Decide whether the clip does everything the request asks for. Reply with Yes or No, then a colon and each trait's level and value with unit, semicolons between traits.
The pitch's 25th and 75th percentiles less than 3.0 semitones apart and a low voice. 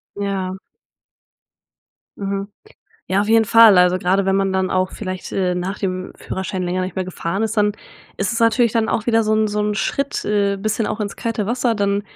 No: narrow, 2.6 semitones; high, 200 Hz